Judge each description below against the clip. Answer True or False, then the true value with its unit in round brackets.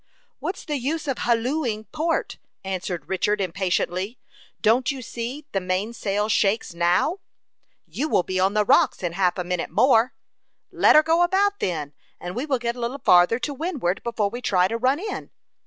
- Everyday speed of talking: True (180 wpm)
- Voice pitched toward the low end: False (230 Hz)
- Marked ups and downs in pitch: True (6.7 semitones)